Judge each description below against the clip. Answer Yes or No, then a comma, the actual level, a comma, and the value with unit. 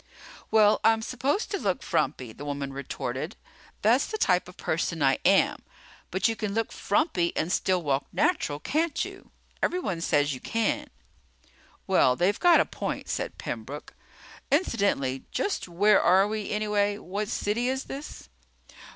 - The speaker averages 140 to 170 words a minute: Yes, average, 150 wpm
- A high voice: Yes, high, 205 Hz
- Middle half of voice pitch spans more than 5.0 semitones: Yes, wide, 5.4 semitones